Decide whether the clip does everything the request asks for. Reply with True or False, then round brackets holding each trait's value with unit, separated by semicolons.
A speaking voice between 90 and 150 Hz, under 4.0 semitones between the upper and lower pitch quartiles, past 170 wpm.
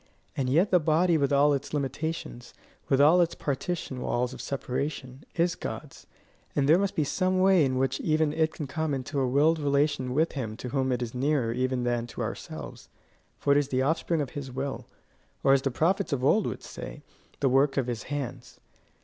True (140 Hz; 3.4 semitones; 205 wpm)